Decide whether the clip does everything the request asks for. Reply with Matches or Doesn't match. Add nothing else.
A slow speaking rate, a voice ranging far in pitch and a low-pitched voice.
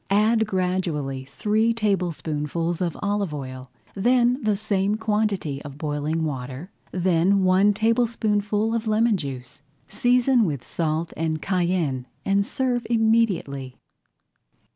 Doesn't match